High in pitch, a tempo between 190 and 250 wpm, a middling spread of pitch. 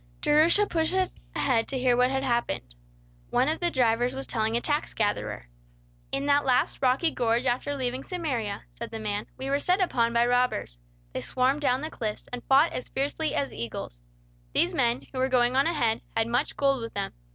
Yes: very high, 255 Hz; average, 195 wpm; average, 3.5 semitones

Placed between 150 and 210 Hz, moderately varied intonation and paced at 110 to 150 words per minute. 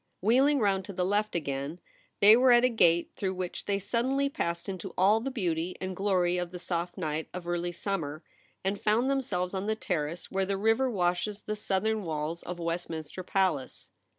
No: high, 190 Hz; average, 3.6 semitones; average, 195 wpm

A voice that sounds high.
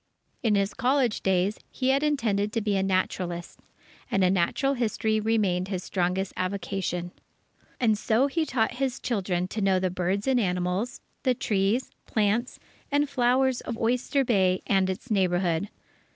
Yes: high, 205 Hz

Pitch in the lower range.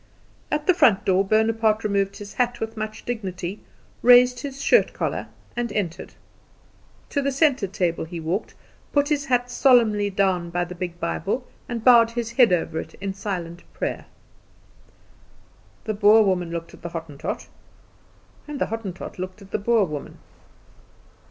No: high, 210 Hz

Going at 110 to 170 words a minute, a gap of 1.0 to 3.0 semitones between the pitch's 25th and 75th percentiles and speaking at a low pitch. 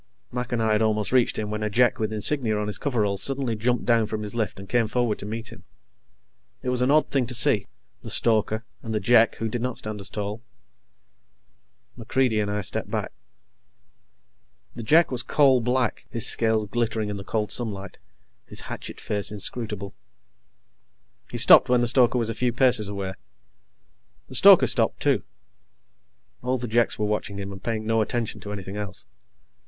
No: average, 190 wpm; average, 2.7 semitones; low, 110 Hz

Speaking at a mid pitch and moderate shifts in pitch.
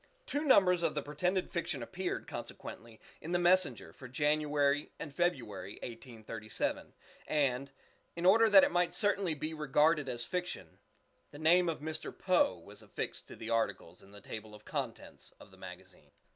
No: medium, 150 Hz; wide, 6.7 semitones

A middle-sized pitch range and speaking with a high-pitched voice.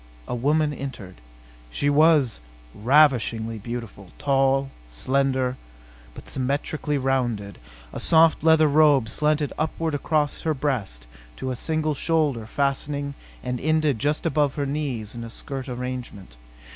No: average, 3.7 semitones; low, 135 Hz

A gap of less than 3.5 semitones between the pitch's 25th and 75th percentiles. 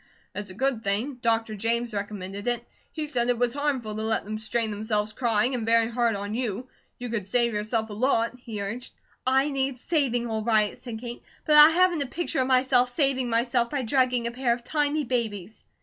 Yes: average, 3.0 semitones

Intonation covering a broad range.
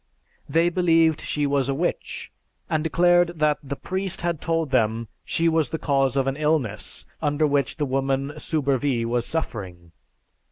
No: average, 3.4 semitones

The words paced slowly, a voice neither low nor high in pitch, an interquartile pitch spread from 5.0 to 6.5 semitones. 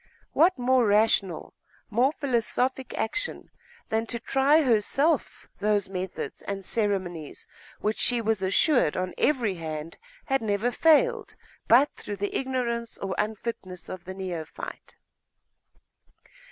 No: slow, 120 wpm; high, 220 Hz; average, 5.3 semitones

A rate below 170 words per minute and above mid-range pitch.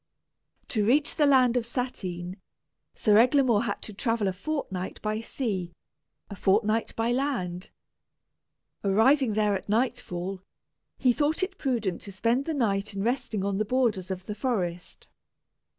Yes: average, 150 wpm; high, 220 Hz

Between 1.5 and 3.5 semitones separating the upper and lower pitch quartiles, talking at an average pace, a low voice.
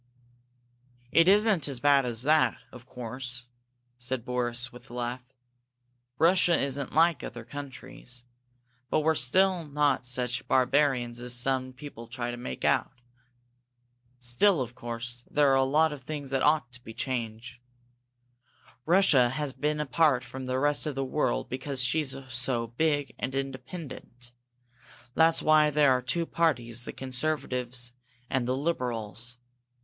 Yes: average, 3.2 semitones; average, 145 wpm; low, 130 Hz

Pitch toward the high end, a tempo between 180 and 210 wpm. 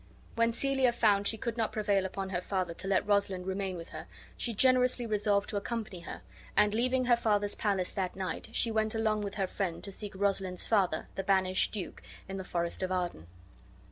Yes: high, 200 Hz; fast, 205 wpm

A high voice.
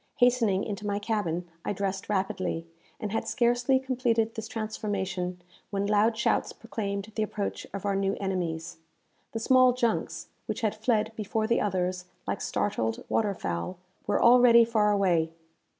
Yes: high, 205 Hz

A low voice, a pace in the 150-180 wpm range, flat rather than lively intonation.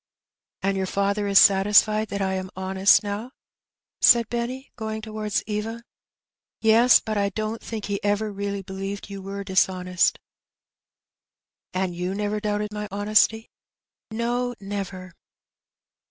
No: high, 205 Hz; average, 155 wpm; narrow, 2.0 semitones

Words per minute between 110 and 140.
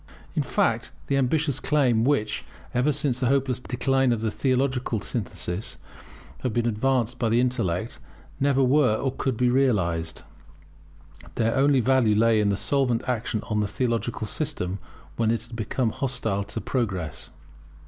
No: average, 155 wpm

